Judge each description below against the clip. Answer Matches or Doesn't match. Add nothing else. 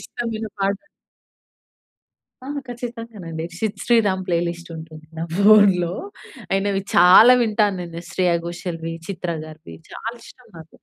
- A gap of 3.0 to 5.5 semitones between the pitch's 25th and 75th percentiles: Matches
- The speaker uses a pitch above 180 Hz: Matches